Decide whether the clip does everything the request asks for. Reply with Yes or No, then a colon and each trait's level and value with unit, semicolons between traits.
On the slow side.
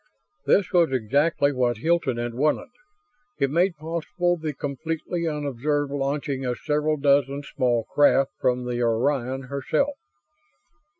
Yes: slow, 125 wpm